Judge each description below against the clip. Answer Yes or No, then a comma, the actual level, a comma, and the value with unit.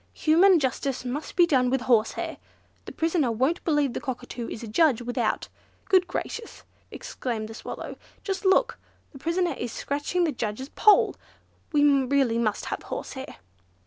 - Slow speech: No, average, 155 wpm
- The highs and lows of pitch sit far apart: Yes, wide, 5.7 semitones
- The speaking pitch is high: Yes, very high, 275 Hz